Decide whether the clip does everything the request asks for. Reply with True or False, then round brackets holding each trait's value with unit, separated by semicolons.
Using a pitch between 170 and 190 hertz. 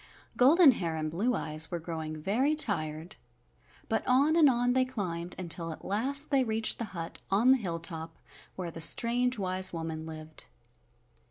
True (185 Hz)